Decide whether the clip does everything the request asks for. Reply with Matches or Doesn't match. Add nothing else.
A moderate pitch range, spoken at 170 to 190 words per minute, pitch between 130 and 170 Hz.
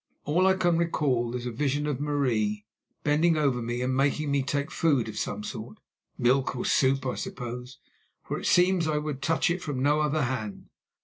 Matches